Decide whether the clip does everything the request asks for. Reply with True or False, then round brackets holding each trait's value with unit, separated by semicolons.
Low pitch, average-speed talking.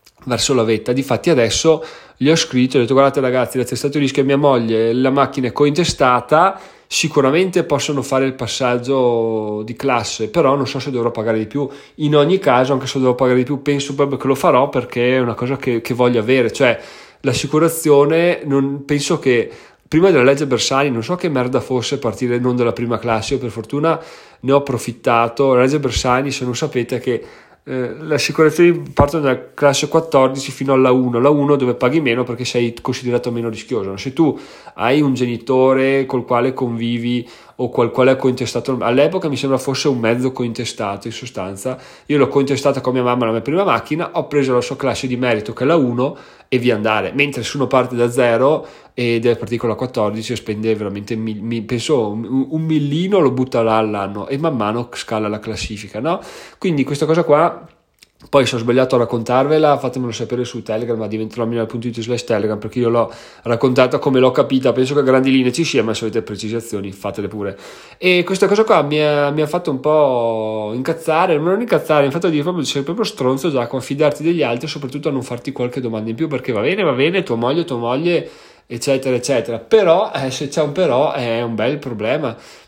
False (130 Hz; 210 wpm)